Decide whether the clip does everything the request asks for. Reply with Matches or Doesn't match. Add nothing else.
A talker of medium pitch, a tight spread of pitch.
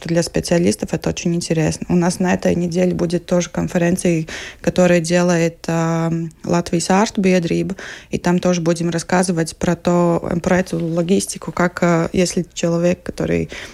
Matches